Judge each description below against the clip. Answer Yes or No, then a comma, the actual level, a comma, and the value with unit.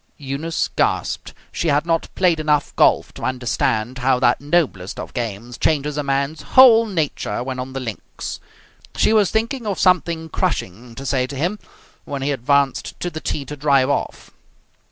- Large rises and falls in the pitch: No, average, 4.4 semitones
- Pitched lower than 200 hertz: Yes, medium, 140 Hz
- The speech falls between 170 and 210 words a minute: Yes, average, 175 wpm